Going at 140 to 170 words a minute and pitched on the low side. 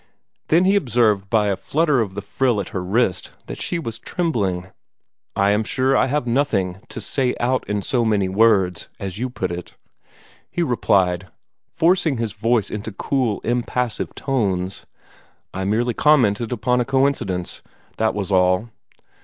Yes: average, 160 wpm; low, 110 Hz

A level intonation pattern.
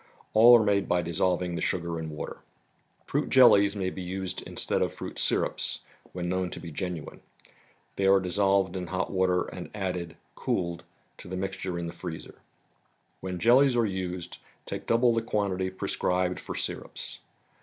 Yes: narrow, 1.9 semitones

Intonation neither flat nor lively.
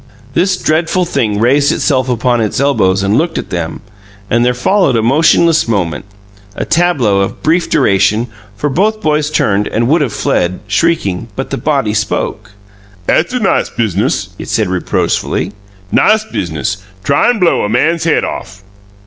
No: wide, 8.1 semitones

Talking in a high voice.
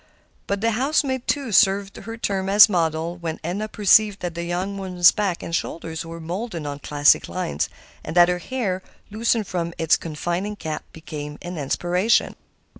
No: medium, 180 Hz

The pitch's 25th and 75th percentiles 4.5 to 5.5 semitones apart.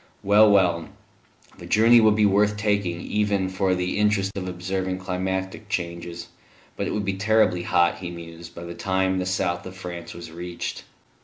No: narrow, 2.6 semitones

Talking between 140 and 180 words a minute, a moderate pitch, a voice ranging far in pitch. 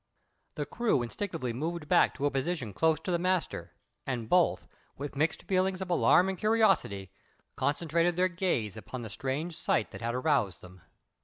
Yes: average, 170 wpm; medium, 155 Hz; wide, 6.9 semitones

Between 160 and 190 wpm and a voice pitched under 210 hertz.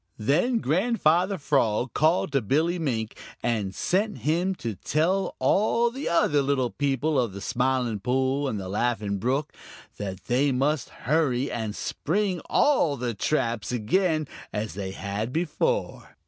No: average, 145 wpm; low, 135 Hz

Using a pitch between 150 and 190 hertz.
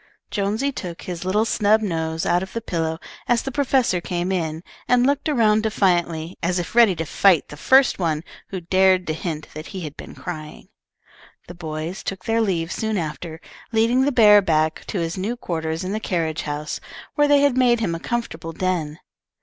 Yes: medium, 185 Hz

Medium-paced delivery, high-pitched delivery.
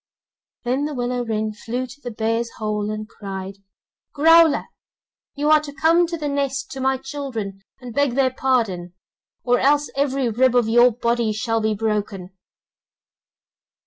Yes: average, 155 wpm; high, 245 Hz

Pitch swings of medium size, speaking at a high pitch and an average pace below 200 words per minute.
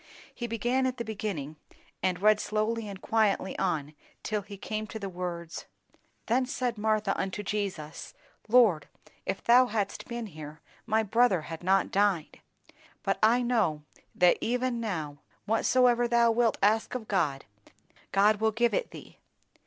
Yes: average, 4.0 semitones; high, 215 Hz; average, 155 wpm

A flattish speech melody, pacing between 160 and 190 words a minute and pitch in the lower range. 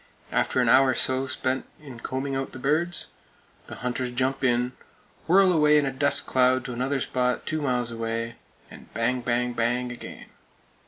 Yes: narrow, 1.8 semitones; average, 175 wpm; low, 130 Hz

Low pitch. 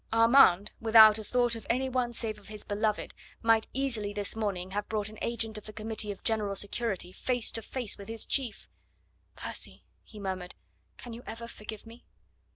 No: high, 220 Hz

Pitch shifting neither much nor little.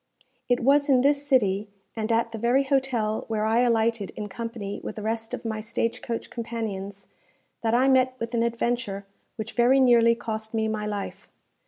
No: narrow, 2.1 semitones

